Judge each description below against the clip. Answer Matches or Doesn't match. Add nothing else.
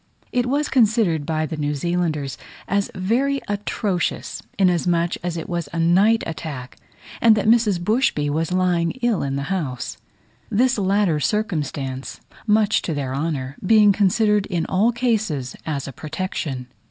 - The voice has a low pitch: Doesn't match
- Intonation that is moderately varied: Doesn't match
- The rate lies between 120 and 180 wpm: Matches